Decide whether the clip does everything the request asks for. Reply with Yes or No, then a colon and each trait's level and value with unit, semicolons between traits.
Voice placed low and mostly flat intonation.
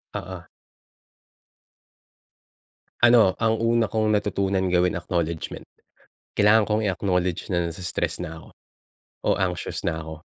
No: very low, 95 Hz; average, 3.6 semitones